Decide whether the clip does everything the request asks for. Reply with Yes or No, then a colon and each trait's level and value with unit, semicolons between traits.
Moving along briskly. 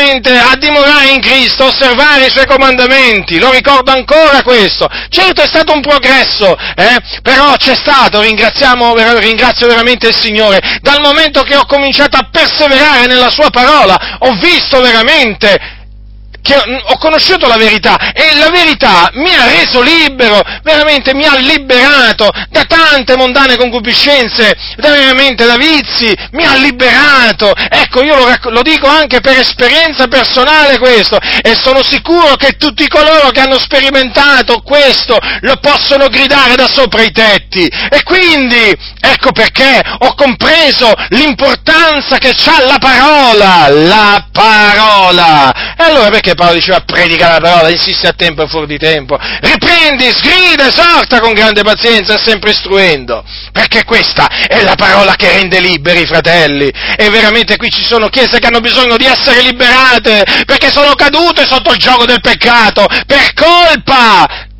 No: average, 150 wpm